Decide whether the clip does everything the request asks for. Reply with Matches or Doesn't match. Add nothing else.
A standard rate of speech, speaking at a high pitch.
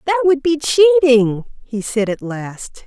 Matches